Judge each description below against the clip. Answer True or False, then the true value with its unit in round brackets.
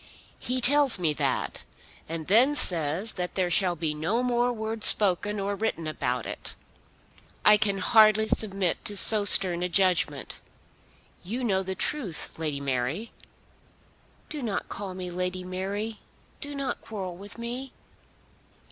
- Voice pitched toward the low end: False (195 Hz)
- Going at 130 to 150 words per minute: True (145 wpm)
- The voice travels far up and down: False (4.0 semitones)